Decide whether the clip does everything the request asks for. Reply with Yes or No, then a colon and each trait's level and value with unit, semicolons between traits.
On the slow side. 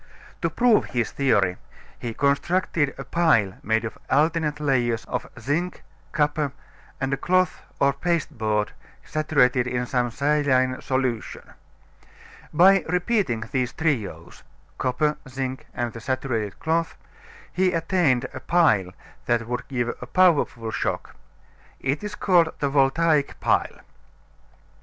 Yes: slow, 125 wpm